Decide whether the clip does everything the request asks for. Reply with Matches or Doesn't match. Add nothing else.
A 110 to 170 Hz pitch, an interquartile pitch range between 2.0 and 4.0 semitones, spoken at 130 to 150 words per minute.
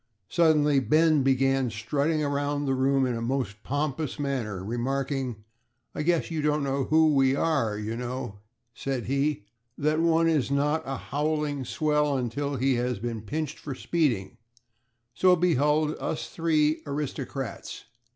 Matches